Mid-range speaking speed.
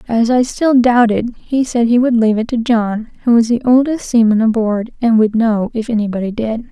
No: fast, 215 wpm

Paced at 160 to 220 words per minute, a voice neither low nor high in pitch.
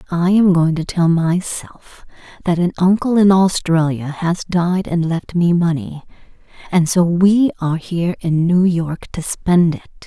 Yes: average, 165 wpm; medium, 175 Hz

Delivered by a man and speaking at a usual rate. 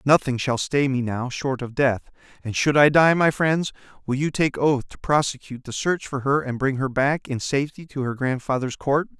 No: male; fast, 220 wpm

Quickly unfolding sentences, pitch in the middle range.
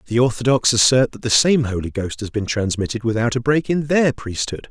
No: fast, 215 wpm; low, 120 Hz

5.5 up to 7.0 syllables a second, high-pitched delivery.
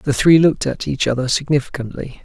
No: 5.9 syllables/s; medium, 140 Hz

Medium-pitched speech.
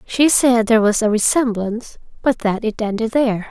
No: high, 225 Hz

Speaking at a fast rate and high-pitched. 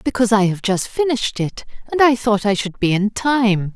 Yes: fast, 225 wpm; high, 215 Hz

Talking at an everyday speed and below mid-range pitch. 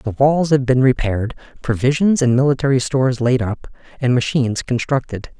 Yes: average, 155 wpm; low, 130 Hz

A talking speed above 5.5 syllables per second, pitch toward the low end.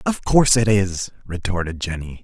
No: 5.1 syllables/s; low, 100 Hz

